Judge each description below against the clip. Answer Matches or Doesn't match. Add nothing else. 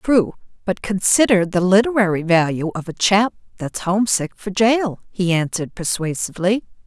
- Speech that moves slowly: Matches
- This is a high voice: Matches